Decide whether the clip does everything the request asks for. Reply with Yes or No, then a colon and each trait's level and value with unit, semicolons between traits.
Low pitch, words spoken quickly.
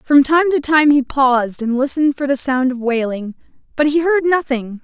No: very high, 275 Hz; fast, 210 wpm